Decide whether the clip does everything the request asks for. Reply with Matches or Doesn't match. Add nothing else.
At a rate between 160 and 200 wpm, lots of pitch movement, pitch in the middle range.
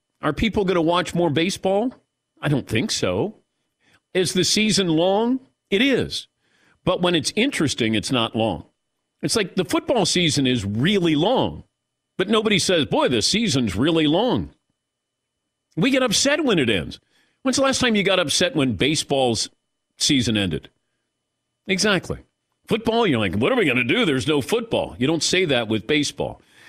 Matches